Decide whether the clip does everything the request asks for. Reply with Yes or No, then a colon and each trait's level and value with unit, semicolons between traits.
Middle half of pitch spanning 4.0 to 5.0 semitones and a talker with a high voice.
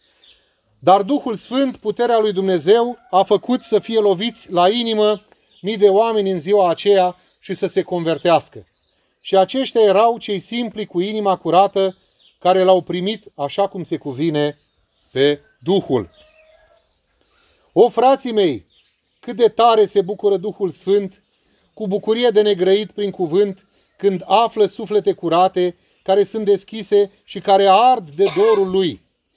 No: average, 3.1 semitones; high, 200 Hz